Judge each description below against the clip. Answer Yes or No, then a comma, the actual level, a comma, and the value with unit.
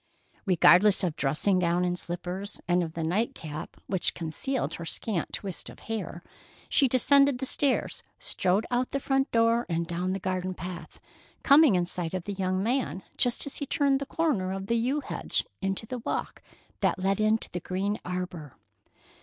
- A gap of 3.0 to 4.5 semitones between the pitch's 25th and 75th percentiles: No, average, 5.2 semitones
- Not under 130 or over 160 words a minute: No, average, 180 wpm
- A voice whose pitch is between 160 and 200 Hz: Yes, high, 190 Hz